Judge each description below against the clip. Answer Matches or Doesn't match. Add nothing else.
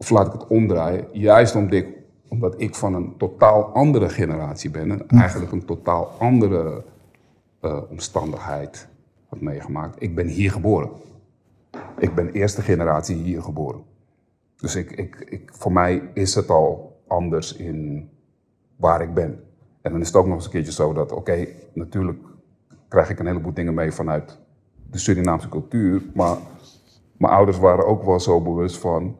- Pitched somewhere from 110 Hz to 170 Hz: Doesn't match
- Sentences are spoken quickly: Doesn't match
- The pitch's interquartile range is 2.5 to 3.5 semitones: Doesn't match